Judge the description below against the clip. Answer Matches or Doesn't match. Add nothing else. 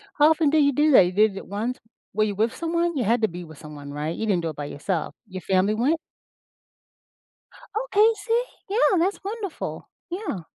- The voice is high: Matches